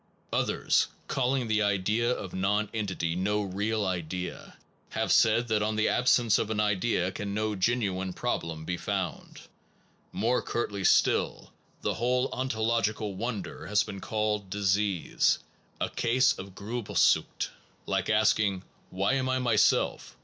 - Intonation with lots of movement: No, average, 3.2 semitones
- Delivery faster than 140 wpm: No, slow, 135 wpm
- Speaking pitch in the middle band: No, low, 105 Hz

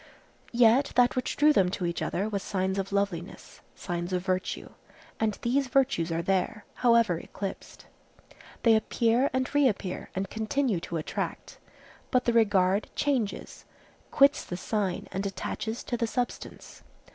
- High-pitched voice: Yes, high, 215 Hz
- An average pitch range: Yes, average, 4.7 semitones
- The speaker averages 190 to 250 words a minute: No, average, 145 wpm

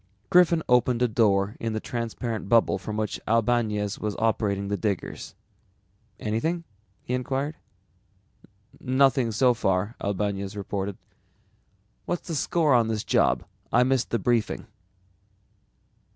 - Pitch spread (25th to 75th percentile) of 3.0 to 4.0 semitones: Yes, average, 3.4 semitones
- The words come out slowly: Yes, slow, 125 wpm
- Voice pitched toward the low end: Yes, low, 115 Hz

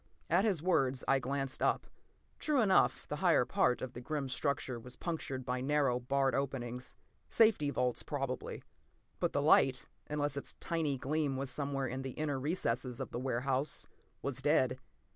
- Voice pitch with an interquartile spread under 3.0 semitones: Yes, narrow, 2.6 semitones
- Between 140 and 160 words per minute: No, average, 170 wpm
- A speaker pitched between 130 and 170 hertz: Yes, low, 135 Hz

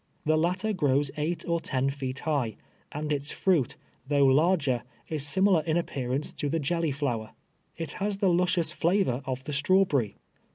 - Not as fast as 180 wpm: Yes, average, 170 wpm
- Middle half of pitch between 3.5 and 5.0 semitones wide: Yes, average, 4.1 semitones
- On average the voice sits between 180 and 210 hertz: No, medium, 150 Hz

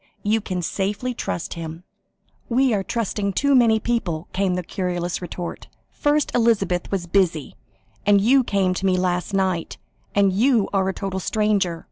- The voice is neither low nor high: No, high, 195 Hz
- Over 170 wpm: No, average, 160 wpm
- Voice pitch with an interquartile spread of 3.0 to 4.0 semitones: Yes, average, 3.5 semitones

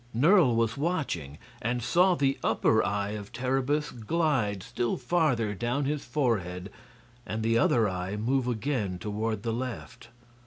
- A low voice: Yes, low, 120 Hz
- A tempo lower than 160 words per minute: Yes, average, 145 wpm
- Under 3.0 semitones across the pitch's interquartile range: No, average, 4.5 semitones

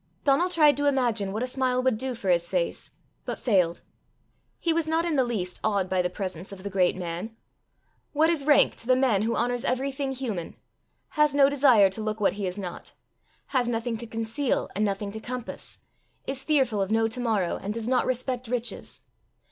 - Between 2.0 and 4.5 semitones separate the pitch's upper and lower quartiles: No, average, 5.0 semitones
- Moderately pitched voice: No, high, 235 Hz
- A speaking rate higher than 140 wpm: Yes, fast, 205 wpm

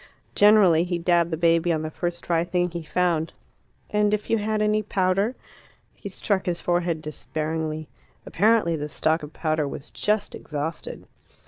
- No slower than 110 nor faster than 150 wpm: No, average, 160 wpm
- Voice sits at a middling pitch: Yes, medium, 170 Hz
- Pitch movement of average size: Yes, average, 3.9 semitones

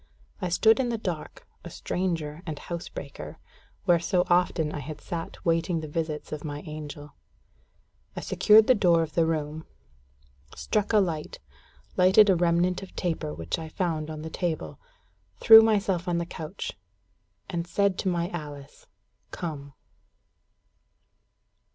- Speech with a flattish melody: No, average, 3.0 semitones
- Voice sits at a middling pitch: Yes, medium, 170 Hz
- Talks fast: No, average, 145 wpm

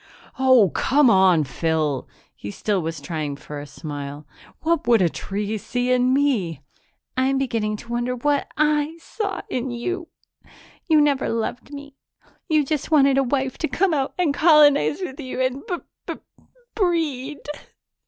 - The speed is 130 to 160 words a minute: Yes, average, 155 wpm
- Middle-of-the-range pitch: No, very high, 260 Hz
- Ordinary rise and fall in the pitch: No, wide, 6.6 semitones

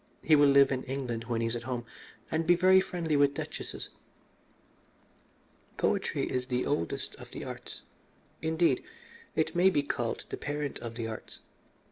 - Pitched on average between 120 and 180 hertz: Yes, medium, 140 Hz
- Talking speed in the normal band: Yes, average, 165 wpm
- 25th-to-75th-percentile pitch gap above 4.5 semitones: Yes, average, 4.9 semitones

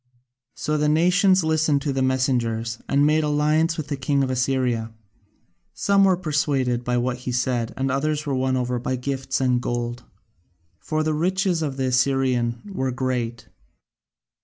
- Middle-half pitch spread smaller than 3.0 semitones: No, average, 3.6 semitones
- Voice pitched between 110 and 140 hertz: Yes, low, 135 Hz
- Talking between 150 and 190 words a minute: Yes, average, 160 wpm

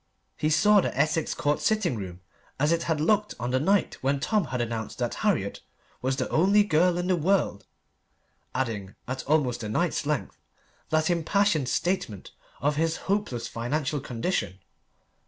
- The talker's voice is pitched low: No, medium, 150 Hz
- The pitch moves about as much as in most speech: No, wide, 6.3 semitones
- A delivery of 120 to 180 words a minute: Yes, average, 160 wpm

